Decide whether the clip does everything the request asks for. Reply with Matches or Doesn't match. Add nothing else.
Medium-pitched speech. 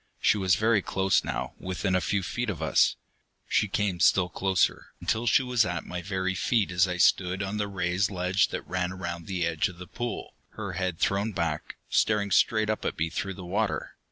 Doesn't match